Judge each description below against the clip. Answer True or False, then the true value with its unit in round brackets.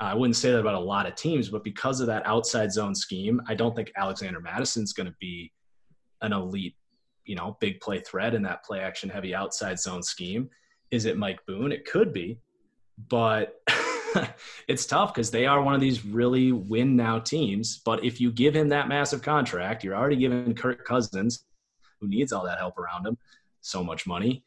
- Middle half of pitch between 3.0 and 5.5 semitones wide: True (3.4 semitones)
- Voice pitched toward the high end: False (115 Hz)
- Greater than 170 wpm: True (200 wpm)